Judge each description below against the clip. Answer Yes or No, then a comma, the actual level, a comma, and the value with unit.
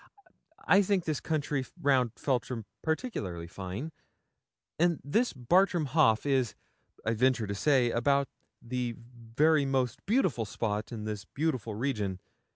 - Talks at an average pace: No, slow, 130 wpm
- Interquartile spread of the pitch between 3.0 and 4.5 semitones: No, average, 5.3 semitones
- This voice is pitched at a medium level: No, low, 130 Hz